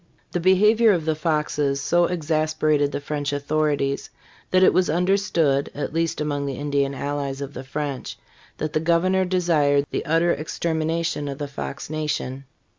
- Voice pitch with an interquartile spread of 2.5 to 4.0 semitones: Yes, average, 2.9 semitones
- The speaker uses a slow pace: No, average, 160 wpm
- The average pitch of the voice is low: No, medium, 155 Hz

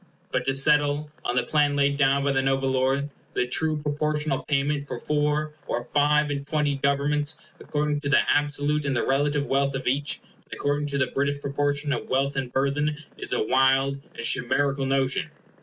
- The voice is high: No, medium, 140 Hz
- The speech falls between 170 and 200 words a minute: Yes, average, 190 wpm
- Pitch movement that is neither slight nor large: No, narrow, 1.5 semitones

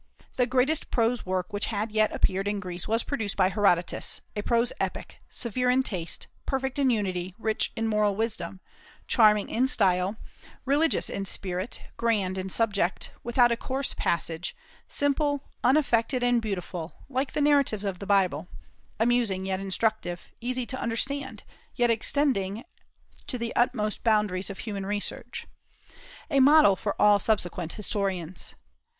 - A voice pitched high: Yes, high, 215 Hz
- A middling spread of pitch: Yes, average, 4.4 semitones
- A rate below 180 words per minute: Yes, average, 145 wpm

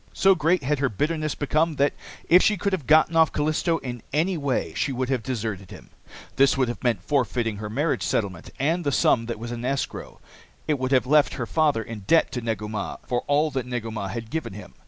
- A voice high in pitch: No, low, 130 Hz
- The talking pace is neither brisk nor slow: No, fast, 230 wpm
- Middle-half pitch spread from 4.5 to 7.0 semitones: Yes, average, 5.1 semitones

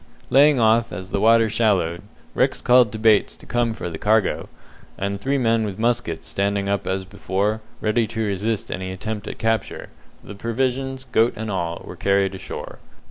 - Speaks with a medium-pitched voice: No, low, 110 Hz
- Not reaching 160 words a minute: No, average, 180 wpm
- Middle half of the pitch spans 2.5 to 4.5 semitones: Yes, average, 2.8 semitones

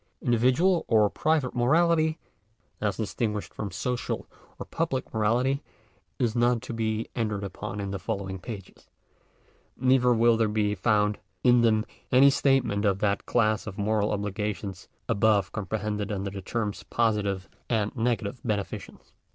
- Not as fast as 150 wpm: Yes, average, 140 wpm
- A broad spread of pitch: No, average, 3.1 semitones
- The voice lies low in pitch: Yes, low, 110 Hz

